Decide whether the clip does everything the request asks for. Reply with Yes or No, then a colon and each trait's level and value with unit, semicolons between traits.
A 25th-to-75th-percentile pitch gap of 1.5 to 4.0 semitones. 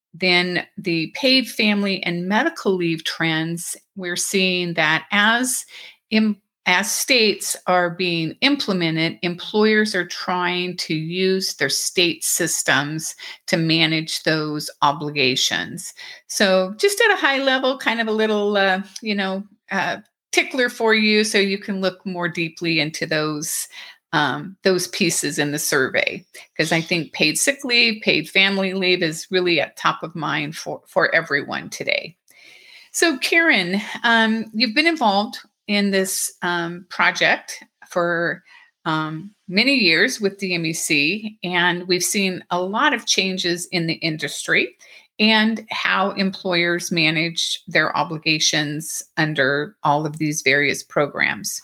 No: average, 4.5 semitones